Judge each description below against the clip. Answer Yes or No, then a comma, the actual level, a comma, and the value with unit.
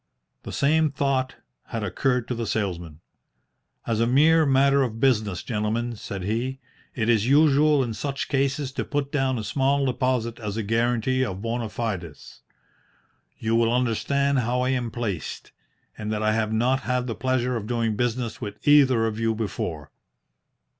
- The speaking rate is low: No, average, 165 wpm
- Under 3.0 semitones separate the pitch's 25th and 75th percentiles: No, average, 3.3 semitones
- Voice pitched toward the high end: No, low, 120 Hz